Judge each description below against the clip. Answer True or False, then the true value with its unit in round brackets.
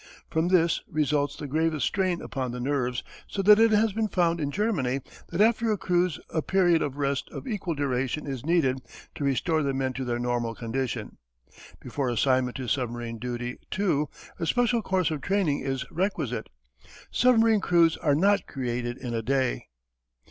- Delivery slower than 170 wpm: False (175 wpm)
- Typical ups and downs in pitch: False (6.1 semitones)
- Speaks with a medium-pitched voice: True (145 Hz)